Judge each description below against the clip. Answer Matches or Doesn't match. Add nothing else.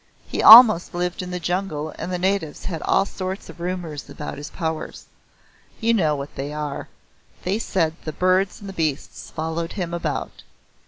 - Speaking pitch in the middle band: Matches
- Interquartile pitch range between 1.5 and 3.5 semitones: Matches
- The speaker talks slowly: Doesn't match